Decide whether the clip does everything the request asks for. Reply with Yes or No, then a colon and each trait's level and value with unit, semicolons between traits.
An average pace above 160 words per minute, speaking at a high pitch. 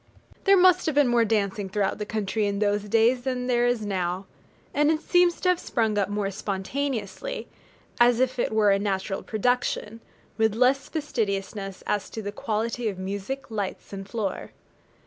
Yes: average, 175 wpm; high, 220 Hz